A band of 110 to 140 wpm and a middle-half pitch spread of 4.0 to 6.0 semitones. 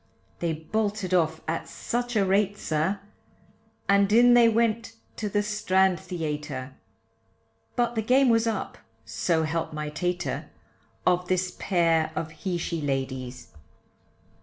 Yes: slow, 135 wpm; average, 5.1 semitones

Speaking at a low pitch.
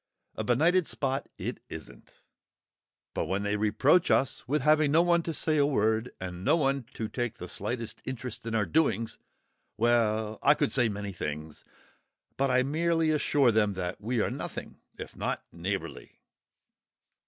Yes: low, 120 Hz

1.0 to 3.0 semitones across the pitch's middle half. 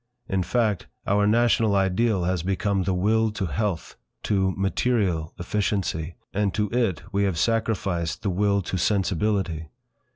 Yes: narrow, 2.6 semitones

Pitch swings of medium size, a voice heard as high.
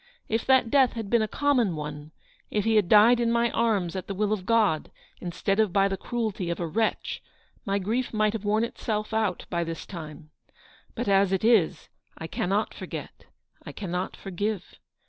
Yes: average, 3.6 semitones; high, 205 Hz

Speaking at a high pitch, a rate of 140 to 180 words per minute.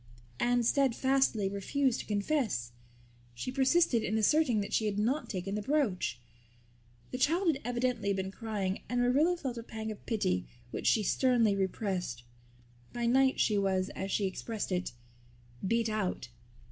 Yes: high, 220 Hz; average, 155 wpm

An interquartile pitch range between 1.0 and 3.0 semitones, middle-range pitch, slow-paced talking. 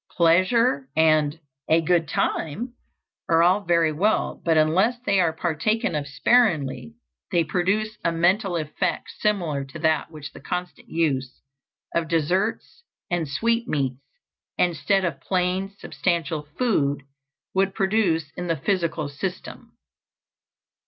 No: average, 3.8 semitones; medium, 170 Hz; slow, 125 wpm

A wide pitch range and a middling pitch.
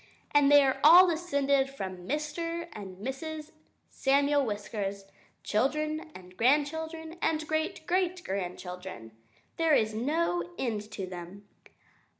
No: wide, 7.8 semitones; very high, 280 Hz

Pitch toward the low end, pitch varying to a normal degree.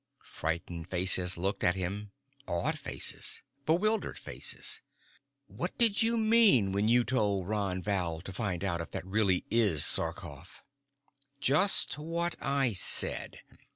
No: low, 100 Hz; wide, 7.4 semitones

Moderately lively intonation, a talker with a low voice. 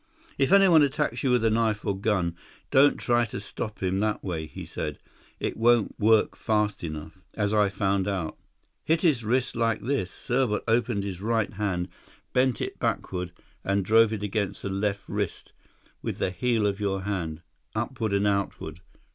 Yes: average, 3.3 semitones; low, 105 Hz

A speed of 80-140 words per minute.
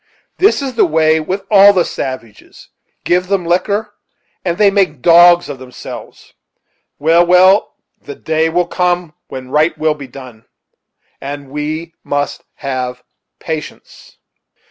Yes: slow, 135 wpm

